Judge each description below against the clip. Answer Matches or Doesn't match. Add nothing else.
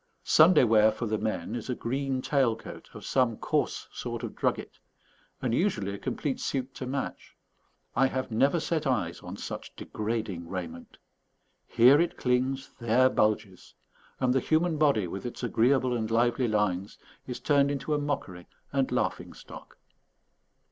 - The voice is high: Doesn't match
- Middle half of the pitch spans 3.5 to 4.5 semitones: Matches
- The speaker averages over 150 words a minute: Matches